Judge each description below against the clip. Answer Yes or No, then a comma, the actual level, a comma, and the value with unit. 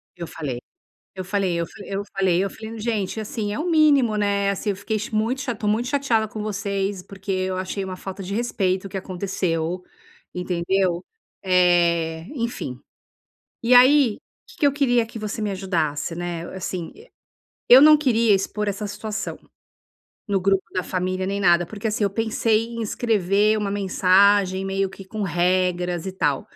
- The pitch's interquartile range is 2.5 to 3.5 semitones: Yes, average, 3.0 semitones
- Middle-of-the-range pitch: No, high, 195 Hz